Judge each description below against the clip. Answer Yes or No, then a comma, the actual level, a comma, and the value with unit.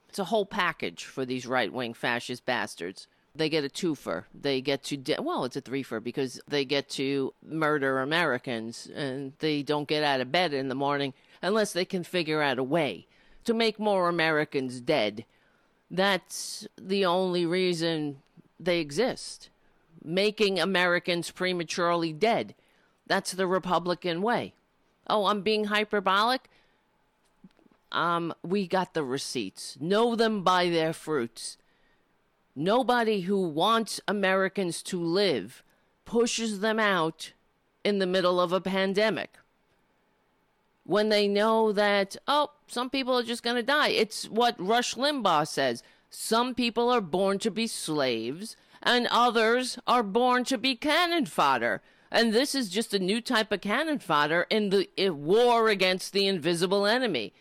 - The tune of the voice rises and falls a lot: Yes, wide, 6.2 semitones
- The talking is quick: No, average, 150 wpm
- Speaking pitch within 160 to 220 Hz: Yes, high, 190 Hz